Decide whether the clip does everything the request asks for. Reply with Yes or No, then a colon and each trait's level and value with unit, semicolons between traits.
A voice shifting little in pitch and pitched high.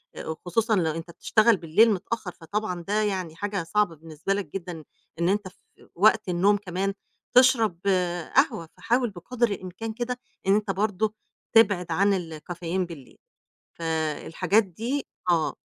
No: average, 4.1 semitones; high, 195 Hz